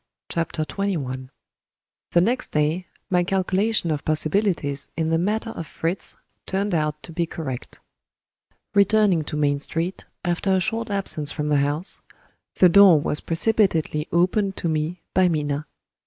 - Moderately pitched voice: Yes, medium, 170 Hz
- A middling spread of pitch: Yes, average, 4.2 semitones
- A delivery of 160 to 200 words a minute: No, average, 145 wpm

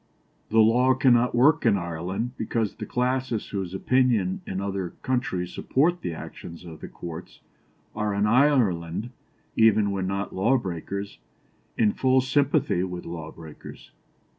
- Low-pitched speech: Yes, low, 105 Hz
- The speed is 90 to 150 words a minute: Yes, average, 140 wpm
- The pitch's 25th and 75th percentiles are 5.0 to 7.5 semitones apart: Yes, wide, 5.5 semitones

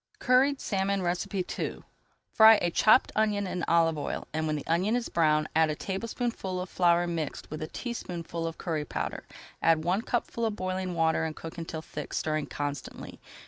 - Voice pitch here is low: No, medium, 175 Hz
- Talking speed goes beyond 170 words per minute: Yes, average, 180 wpm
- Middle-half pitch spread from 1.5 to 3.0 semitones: No, average, 3.9 semitones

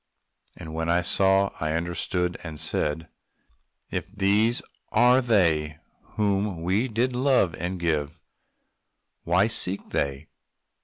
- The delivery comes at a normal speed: No, slow, 115 wpm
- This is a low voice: Yes, very low, 90 Hz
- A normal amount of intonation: Yes, average, 4.3 semitones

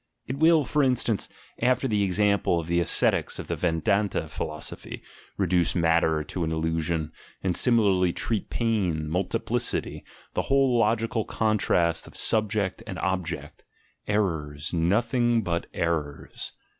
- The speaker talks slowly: Yes, slow, 130 wpm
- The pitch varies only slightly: No, average, 5.2 semitones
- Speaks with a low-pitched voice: Yes, very low, 95 Hz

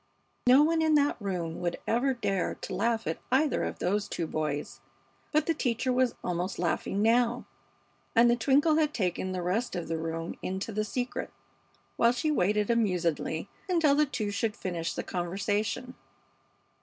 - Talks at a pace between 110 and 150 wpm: No, average, 170 wpm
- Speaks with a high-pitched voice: Yes, high, 220 Hz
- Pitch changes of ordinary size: No, wide, 6.1 semitones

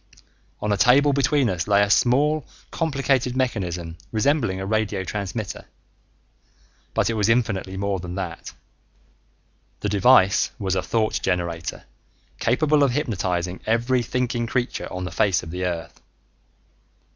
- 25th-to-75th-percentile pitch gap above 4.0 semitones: Yes, average, 5.2 semitones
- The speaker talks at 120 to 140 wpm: Yes, slow, 135 wpm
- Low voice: Yes, low, 105 Hz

